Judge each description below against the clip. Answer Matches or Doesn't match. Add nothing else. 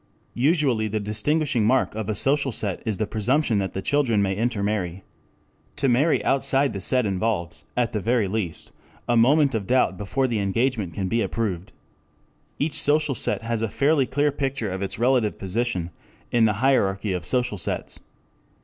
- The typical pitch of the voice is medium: Doesn't match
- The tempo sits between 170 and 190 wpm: Matches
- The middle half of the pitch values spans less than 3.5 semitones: Doesn't match